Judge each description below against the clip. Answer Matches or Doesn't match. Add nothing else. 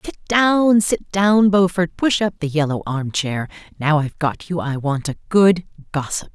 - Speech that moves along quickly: Doesn't match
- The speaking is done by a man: Doesn't match